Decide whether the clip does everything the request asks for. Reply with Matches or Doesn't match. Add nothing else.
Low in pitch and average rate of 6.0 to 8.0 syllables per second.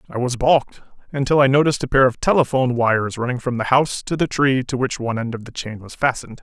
Matches